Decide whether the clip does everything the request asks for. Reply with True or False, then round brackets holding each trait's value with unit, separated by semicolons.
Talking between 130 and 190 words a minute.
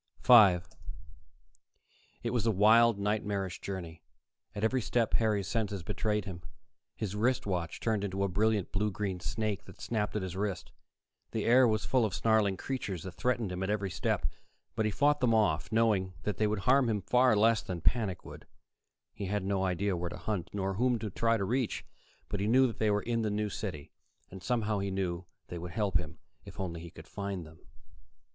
False (200 wpm)